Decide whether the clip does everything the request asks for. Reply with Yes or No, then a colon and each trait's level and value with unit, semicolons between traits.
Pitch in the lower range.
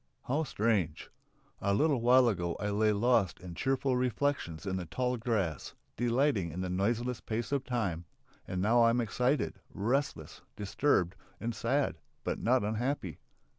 Yes: low, 115 Hz